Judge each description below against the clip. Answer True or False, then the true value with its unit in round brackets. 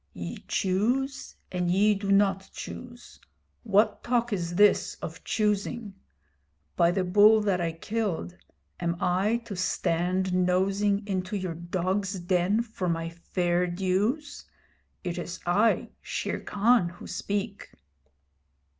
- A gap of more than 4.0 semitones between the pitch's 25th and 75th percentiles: False (2.9 semitones)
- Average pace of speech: False (125 wpm)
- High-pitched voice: True (195 Hz)